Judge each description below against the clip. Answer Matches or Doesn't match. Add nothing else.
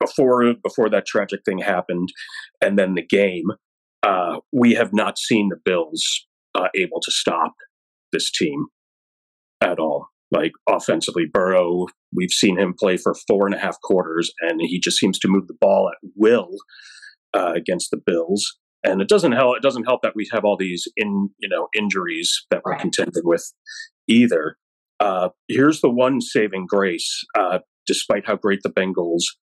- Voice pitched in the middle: Doesn't match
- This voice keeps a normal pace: Matches